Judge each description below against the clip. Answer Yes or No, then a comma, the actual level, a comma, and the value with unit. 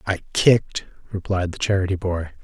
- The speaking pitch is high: No, very low, 95 Hz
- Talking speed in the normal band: Yes, average, 150 wpm